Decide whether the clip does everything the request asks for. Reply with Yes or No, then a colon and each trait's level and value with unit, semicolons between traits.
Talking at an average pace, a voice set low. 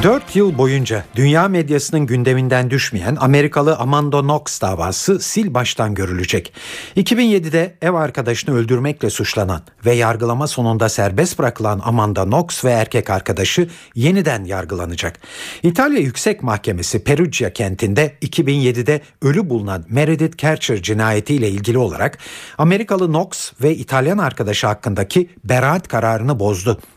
Yes: average, 120 wpm; low, 130 Hz